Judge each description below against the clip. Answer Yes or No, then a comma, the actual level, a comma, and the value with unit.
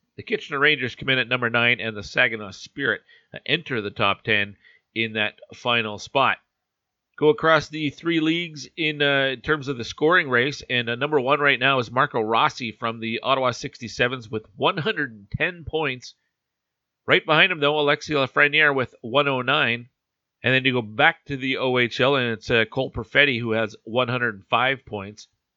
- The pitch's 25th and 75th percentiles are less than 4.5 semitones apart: Yes, average, 4.0 semitones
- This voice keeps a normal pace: Yes, average, 175 wpm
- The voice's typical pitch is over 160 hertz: No, low, 130 Hz